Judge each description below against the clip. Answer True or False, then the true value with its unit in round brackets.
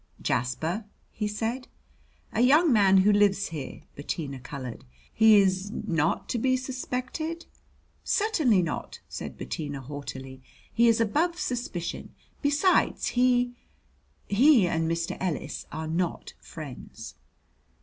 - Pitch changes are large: True (7.6 semitones)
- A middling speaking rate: False (120 wpm)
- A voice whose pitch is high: True (205 Hz)